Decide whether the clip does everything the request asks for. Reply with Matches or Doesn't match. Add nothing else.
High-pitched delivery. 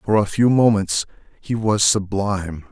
Doesn't match